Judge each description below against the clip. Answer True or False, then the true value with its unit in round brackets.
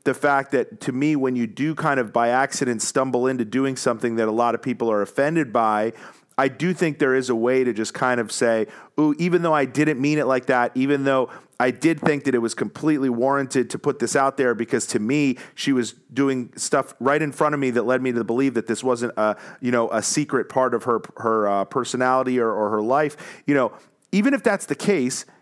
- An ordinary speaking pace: False (240 wpm)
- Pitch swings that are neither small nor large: True (3.0 semitones)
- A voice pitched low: True (130 Hz)